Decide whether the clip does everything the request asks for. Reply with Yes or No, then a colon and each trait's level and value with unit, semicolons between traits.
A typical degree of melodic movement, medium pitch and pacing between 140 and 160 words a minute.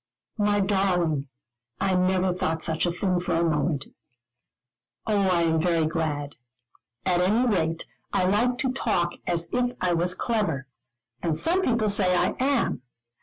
Yes: average, 4.0 semitones; medium, 180 Hz; average, 155 wpm